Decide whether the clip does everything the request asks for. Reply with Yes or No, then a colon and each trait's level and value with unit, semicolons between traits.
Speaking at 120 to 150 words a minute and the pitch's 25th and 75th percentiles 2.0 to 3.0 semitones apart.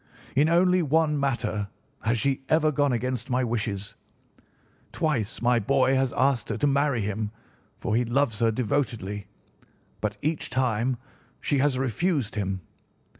No: average, 145 wpm; average, 4.3 semitones